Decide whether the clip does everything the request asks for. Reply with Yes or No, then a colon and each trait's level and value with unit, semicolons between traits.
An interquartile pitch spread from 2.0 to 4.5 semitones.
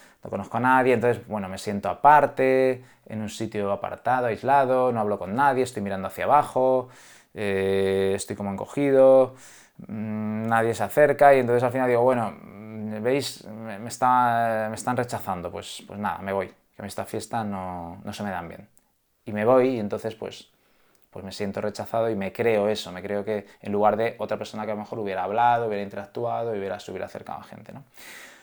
Yes: average, 3.7 semitones